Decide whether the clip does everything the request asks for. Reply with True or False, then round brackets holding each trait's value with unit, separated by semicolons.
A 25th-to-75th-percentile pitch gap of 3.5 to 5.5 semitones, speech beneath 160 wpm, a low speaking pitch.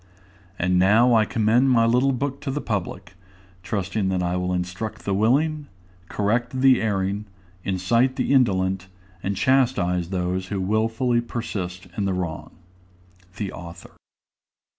True (4.8 semitones; 140 wpm; 105 Hz)